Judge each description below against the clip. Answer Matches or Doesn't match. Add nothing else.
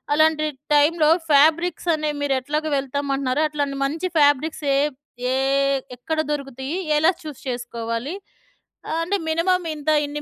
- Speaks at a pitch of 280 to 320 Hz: Matches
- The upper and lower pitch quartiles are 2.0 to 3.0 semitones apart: Matches